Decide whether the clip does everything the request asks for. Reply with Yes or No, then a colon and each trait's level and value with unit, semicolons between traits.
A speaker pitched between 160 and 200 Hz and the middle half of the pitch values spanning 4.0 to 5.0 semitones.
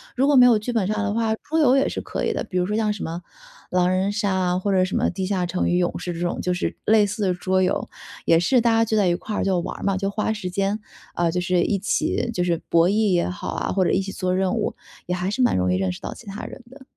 No: high, 190 Hz; average, 3.0 semitones